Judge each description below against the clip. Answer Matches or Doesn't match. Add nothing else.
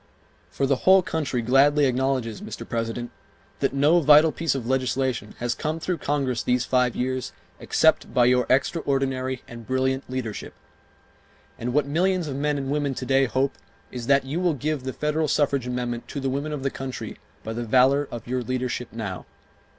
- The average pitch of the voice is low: Matches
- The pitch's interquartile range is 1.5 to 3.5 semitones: Matches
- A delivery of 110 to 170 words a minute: Doesn't match